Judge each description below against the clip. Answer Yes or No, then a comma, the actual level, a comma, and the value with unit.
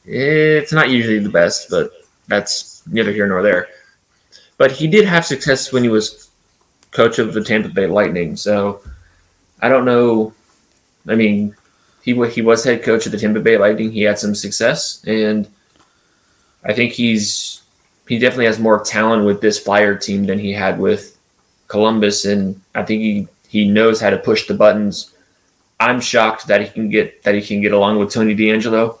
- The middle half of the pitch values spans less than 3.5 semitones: Yes, narrow, 2.6 semitones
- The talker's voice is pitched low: Yes, low, 110 Hz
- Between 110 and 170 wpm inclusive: No, average, 180 wpm